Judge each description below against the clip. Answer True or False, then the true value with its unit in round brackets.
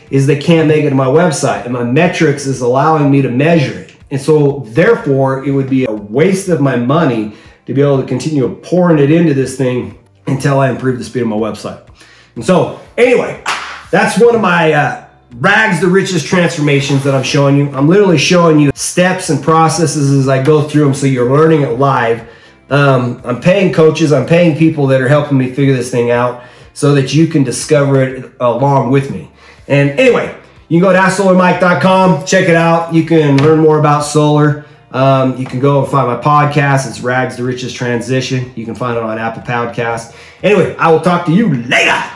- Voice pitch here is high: False (140 Hz)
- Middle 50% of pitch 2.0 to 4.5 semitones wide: True (3.9 semitones)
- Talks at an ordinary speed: False (210 wpm)